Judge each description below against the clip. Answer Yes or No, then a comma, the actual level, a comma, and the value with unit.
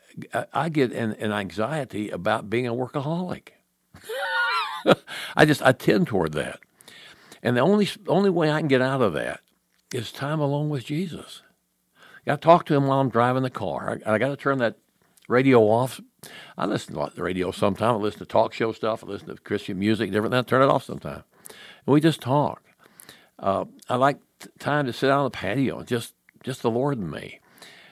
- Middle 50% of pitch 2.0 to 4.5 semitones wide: No, average, 5.1 semitones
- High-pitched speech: No, low, 130 Hz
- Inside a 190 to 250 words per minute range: Yes, fast, 205 wpm